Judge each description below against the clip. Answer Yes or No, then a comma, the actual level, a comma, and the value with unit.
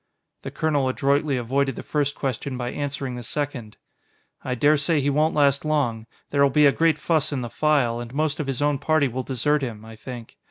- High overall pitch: No, medium, 140 Hz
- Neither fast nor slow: No, fast, 210 wpm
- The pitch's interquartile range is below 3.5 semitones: Yes, average, 2.9 semitones